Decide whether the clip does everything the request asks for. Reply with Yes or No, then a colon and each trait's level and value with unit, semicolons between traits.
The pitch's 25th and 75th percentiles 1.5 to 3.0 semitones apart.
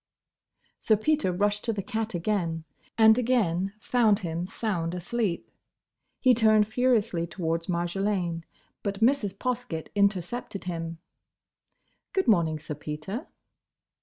No: average, 4.8 semitones